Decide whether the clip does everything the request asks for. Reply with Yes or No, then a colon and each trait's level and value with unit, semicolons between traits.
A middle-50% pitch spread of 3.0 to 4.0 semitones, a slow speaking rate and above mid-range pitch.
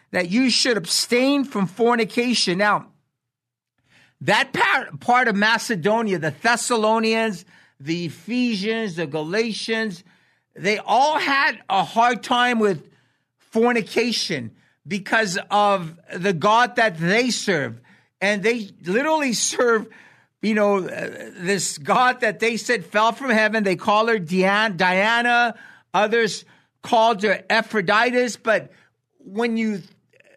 Yes: average, 3.7 semitones; slow, 115 wpm; high, 215 Hz